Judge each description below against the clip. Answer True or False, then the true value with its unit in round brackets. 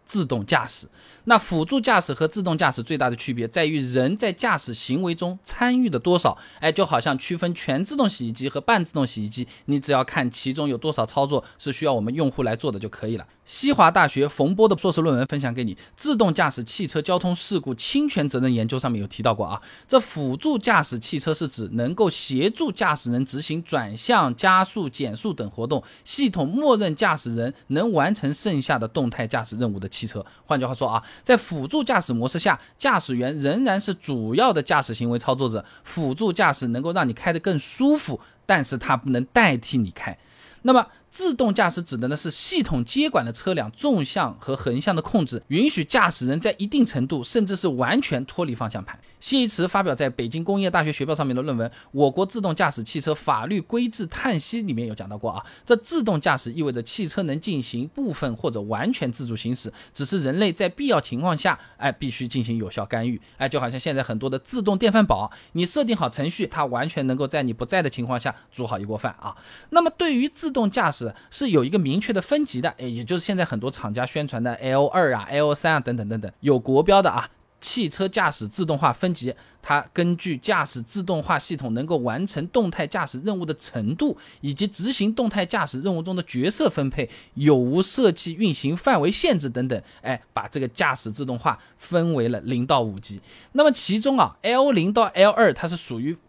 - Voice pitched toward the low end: False (150 Hz)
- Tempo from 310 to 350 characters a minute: True (320 characters per minute)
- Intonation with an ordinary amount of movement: False (7.5 semitones)